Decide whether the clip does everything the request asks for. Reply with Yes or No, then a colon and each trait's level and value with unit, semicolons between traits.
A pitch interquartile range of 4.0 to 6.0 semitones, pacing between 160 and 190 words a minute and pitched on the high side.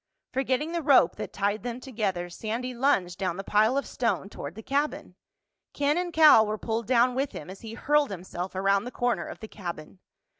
No: average, 5.3 semitones; average, 200 wpm; high, 225 Hz